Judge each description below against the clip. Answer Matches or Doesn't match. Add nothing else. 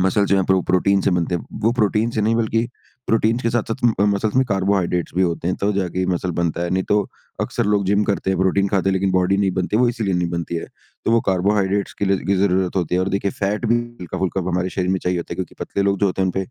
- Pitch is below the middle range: Matches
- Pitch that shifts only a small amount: Matches